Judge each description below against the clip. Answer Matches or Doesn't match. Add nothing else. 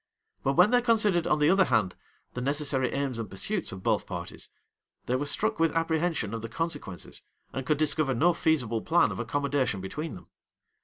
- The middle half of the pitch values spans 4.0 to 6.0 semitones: Matches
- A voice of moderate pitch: Matches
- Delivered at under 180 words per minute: Doesn't match